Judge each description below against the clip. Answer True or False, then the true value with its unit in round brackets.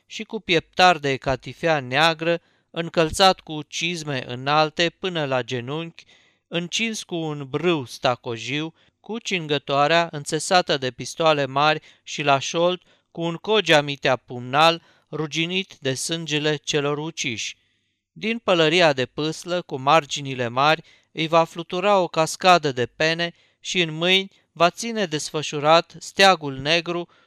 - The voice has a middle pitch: True (160 Hz)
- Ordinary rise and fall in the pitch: True (3.4 semitones)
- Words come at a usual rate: True (130 wpm)